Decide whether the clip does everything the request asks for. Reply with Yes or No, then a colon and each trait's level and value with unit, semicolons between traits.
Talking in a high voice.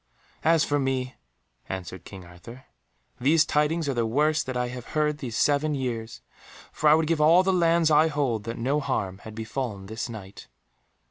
No: low, 135 Hz